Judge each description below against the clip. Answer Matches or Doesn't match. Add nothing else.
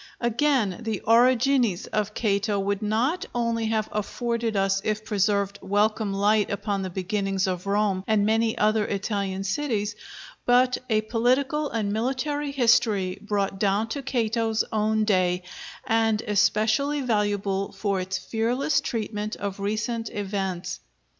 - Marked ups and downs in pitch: Doesn't match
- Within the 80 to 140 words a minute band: Matches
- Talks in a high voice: Matches